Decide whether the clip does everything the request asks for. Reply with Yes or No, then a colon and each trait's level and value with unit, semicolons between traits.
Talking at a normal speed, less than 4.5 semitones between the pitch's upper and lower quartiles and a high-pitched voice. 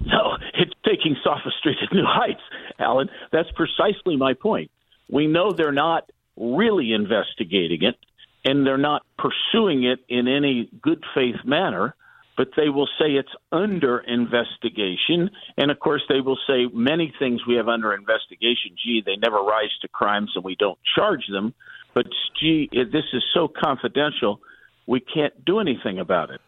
No: average, 165 wpm; average, 3.9 semitones; low, 135 Hz